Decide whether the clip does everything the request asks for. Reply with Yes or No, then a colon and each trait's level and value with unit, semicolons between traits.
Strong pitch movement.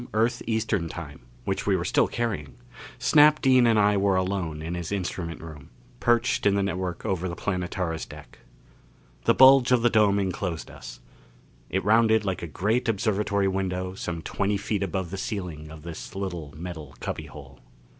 No: average, 4.2 semitones